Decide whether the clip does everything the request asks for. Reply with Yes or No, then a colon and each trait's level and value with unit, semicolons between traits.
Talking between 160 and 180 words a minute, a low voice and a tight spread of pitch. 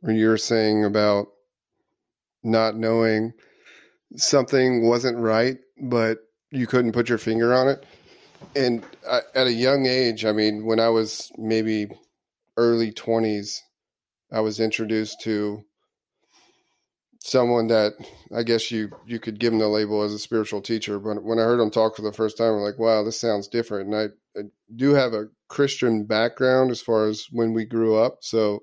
Yes: average, 170 wpm; low, 110 Hz; narrow, 1.6 semitones